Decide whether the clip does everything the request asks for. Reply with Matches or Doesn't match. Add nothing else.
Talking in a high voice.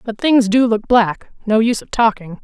Matches